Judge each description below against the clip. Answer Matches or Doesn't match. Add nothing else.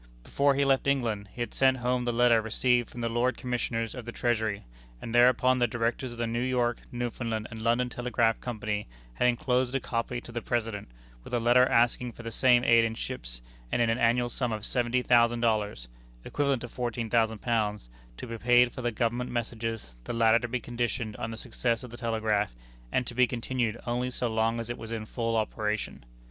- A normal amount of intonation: Doesn't match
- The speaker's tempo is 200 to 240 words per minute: Matches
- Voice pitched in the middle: Doesn't match